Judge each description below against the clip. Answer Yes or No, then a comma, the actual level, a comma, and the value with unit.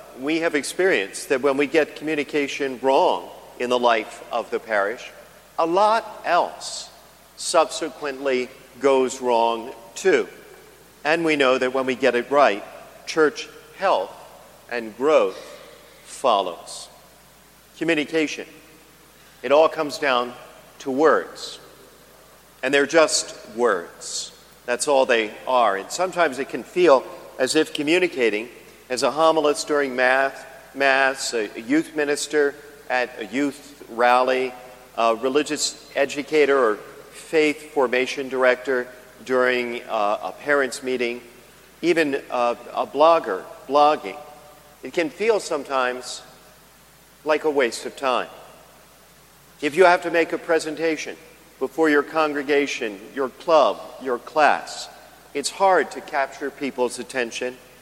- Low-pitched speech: No, medium, 145 Hz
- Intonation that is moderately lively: Yes, average, 3.7 semitones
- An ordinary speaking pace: No, slow, 120 wpm